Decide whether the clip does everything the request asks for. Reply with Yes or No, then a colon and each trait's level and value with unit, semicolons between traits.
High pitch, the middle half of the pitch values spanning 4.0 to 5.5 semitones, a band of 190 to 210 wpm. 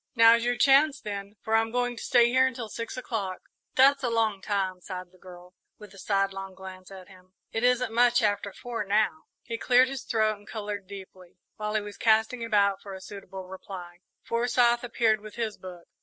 No: high, 215 Hz; average, 3.6 semitones; average, 200 wpm